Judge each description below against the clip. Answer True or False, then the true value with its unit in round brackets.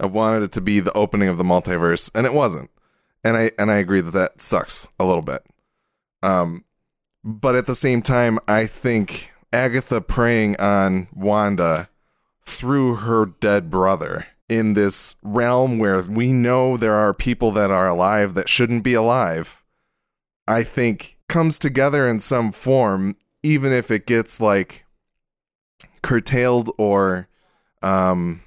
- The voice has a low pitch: True (110 Hz)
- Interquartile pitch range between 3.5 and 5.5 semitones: True (3.9 semitones)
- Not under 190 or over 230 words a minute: False (150 wpm)